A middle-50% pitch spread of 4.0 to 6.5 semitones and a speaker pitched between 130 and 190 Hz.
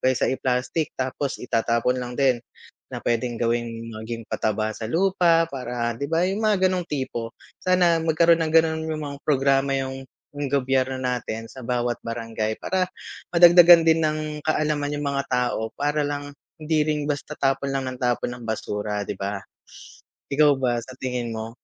Yes: average, 4.5 semitones; low, 135 Hz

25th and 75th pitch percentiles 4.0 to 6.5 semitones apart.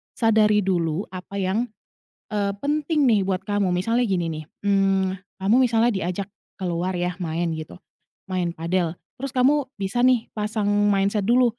No: average, 3.6 semitones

